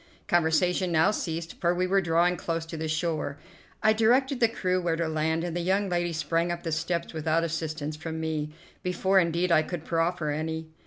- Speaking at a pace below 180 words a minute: No, average, 200 wpm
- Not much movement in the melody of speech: Yes, narrow, 2.0 semitones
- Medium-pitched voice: Yes, medium, 170 Hz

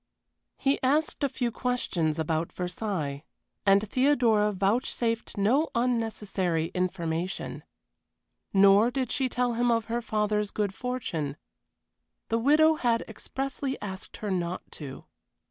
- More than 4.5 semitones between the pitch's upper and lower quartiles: Yes, average, 5.1 semitones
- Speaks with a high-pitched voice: Yes, high, 215 Hz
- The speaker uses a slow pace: Yes, slow, 120 wpm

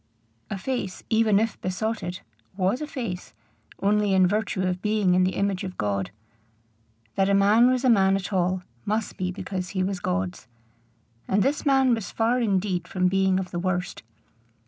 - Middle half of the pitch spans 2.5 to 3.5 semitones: Yes, average, 3.0 semitones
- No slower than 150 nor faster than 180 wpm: Yes, average, 175 wpm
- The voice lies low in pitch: No, high, 195 Hz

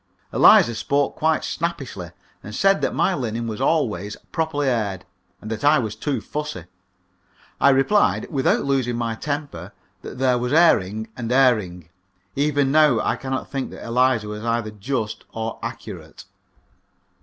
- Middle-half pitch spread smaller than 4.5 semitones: No, average, 4.8 semitones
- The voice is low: Yes, low, 125 Hz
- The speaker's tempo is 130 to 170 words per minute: Yes, average, 150 wpm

